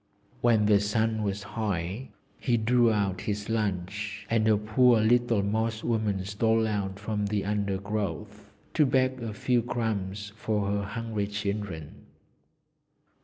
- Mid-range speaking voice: No, low, 105 Hz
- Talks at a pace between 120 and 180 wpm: Yes, slow, 135 wpm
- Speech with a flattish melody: Yes, narrow, 1.9 semitones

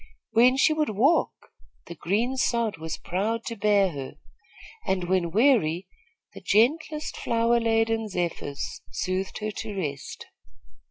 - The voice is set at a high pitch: Yes, high, 215 Hz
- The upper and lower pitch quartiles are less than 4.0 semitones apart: No, average, 4.3 semitones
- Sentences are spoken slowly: Yes, slow, 130 wpm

